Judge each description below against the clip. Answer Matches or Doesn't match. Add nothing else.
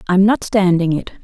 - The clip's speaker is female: Matches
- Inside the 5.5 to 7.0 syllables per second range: Doesn't match